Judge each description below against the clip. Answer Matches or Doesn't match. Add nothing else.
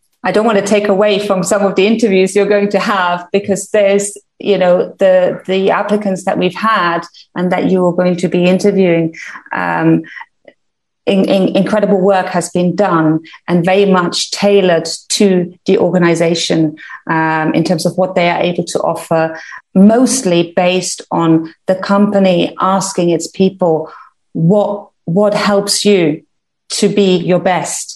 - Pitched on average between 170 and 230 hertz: Matches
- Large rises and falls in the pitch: Doesn't match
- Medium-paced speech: Matches